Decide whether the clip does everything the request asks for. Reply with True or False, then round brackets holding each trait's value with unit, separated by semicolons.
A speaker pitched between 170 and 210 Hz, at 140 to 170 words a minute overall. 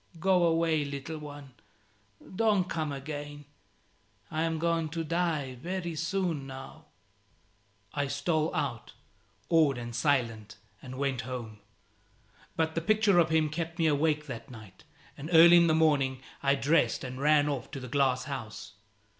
False (150 Hz; 150 wpm)